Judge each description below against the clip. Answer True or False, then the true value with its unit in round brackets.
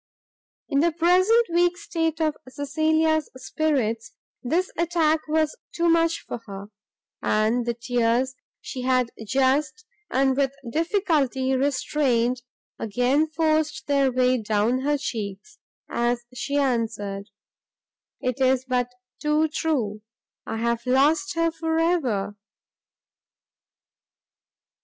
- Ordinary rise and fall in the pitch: True (4.7 semitones)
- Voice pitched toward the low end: False (270 Hz)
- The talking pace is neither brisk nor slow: False (110 wpm)